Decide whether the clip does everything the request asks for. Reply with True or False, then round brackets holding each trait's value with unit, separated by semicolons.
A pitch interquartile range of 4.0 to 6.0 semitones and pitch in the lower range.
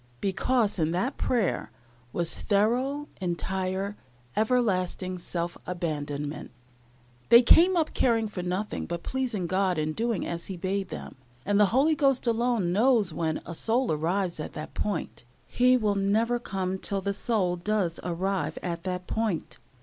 False (4.6 semitones; 195 Hz)